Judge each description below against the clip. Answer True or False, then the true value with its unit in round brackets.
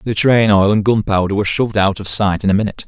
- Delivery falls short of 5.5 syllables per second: False (6.9 syllables/s)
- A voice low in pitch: True (105 Hz)